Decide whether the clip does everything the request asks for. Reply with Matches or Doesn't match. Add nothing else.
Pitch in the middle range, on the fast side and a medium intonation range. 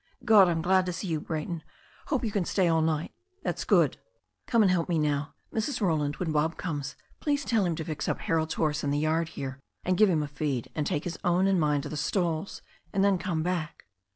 Matches